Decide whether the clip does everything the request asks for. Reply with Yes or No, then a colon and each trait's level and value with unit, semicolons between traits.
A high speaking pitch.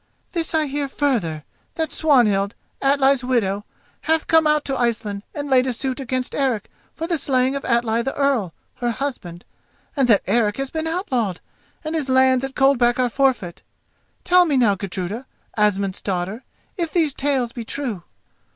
Yes: very high, 255 Hz